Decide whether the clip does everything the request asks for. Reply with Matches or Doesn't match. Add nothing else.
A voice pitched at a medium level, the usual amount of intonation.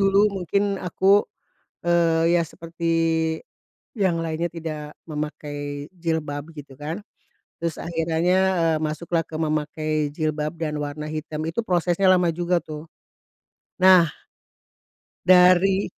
Doesn't match